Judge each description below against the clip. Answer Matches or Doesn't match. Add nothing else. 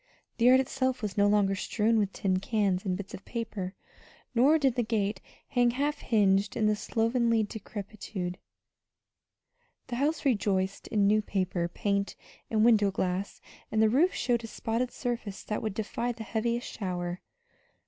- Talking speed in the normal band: Matches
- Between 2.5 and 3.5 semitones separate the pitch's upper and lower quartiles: Matches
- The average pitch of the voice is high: Matches